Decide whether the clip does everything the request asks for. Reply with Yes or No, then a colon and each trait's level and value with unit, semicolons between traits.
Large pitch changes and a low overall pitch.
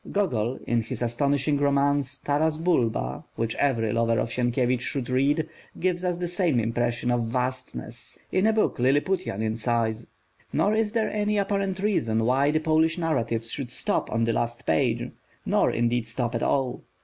Yes: wide, 5.7 semitones; low, 130 Hz